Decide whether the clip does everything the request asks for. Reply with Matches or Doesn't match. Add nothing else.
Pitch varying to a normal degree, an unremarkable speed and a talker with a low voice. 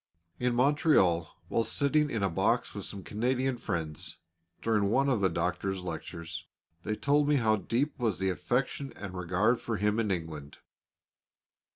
Doesn't match